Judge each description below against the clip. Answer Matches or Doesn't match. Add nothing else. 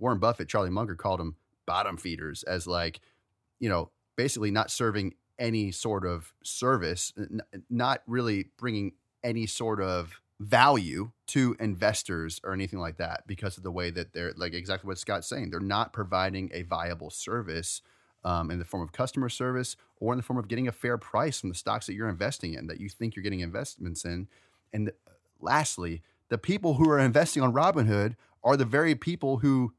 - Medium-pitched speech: Doesn't match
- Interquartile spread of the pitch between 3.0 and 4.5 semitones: Doesn't match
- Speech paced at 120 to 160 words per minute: Doesn't match